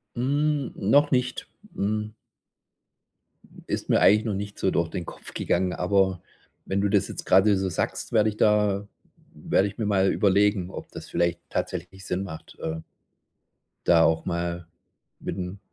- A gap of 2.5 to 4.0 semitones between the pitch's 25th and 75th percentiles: Yes, average, 2.8 semitones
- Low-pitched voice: Yes, low, 100 Hz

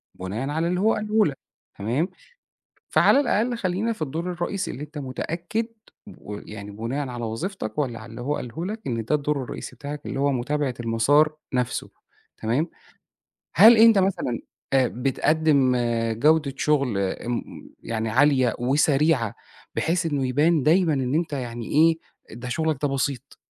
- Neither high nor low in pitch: Yes, medium, 145 Hz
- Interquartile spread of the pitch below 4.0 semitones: No, average, 5.1 semitones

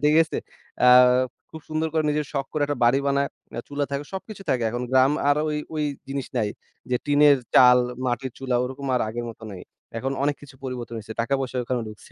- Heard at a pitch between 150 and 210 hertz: No, low, 135 Hz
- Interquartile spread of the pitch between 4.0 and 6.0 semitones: No, average, 2.8 semitones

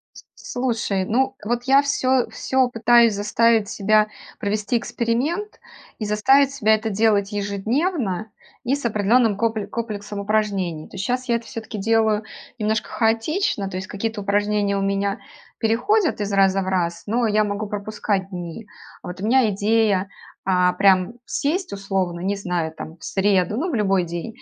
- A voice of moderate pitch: No, high, 210 Hz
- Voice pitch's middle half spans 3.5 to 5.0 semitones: No, average, 2.9 semitones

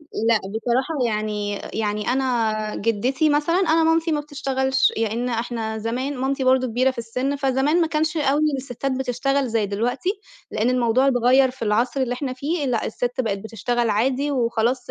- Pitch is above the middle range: Yes, very high, 255 Hz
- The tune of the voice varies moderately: Yes, average, 3.3 semitones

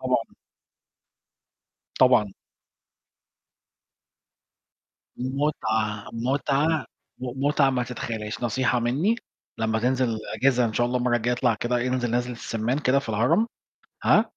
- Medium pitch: No, low, 125 Hz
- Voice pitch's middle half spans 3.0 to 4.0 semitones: No, narrow, 2.4 semitones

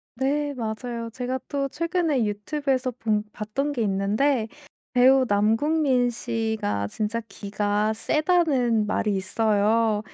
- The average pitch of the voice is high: Yes, high, 230 Hz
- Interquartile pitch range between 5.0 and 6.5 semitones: No, average, 4.3 semitones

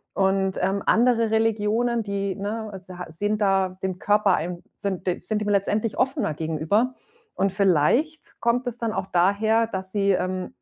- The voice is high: Yes, high, 200 Hz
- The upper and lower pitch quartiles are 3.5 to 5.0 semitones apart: No, average, 2.9 semitones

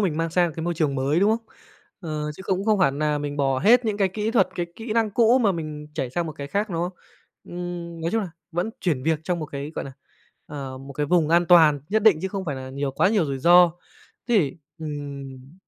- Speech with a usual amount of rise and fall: Yes, average, 4.8 semitones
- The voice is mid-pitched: Yes, medium, 165 Hz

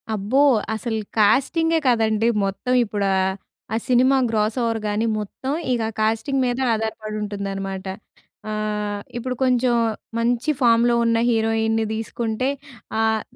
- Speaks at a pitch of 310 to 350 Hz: No, high, 225 Hz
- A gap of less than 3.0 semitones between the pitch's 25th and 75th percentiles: Yes, narrow, 2.4 semitones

